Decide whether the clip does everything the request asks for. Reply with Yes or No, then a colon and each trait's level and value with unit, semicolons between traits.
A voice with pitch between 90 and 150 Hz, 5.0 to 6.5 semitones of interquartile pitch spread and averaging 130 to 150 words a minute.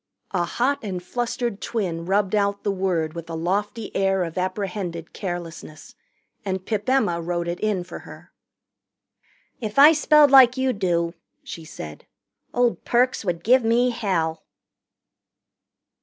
No: high, 195 Hz; average, 5.3 semitones; average, 140 wpm